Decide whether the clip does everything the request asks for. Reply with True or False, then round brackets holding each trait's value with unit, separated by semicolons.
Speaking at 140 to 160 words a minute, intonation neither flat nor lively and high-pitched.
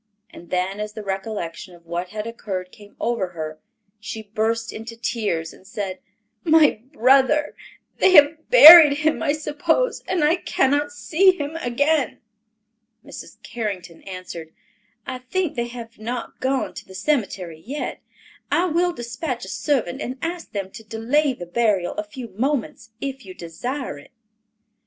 False (150 wpm; 7.1 semitones; 235 Hz)